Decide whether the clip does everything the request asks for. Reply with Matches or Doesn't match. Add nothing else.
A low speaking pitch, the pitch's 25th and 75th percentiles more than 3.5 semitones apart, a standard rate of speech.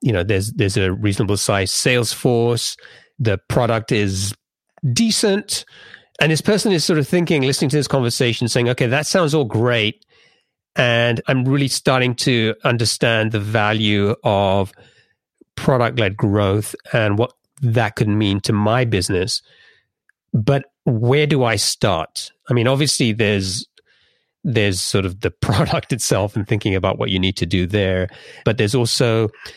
Matches